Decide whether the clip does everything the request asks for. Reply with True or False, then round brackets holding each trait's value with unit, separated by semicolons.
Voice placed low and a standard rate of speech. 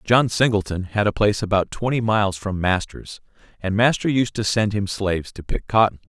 True (105 Hz; 195 wpm)